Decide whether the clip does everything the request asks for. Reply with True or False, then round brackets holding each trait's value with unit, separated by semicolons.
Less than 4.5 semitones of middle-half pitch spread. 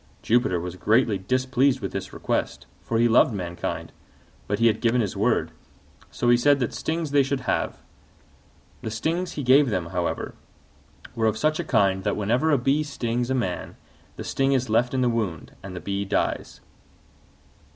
False (4.9 semitones)